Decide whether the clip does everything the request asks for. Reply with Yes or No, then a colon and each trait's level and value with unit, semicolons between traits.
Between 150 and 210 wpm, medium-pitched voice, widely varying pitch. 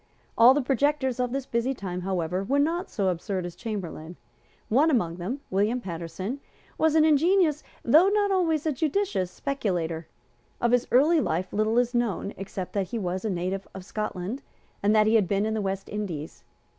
No: average, 185 wpm; high, 220 Hz; wide, 6.9 semitones